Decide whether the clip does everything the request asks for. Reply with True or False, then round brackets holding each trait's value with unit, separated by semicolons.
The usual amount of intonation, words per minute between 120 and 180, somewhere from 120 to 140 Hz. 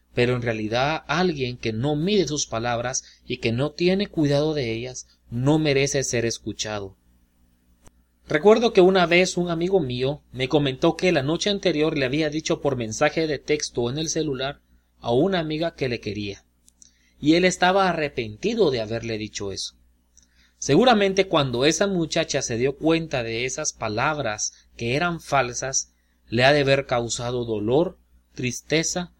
False (6.4 semitones; 160 wpm; 135 Hz)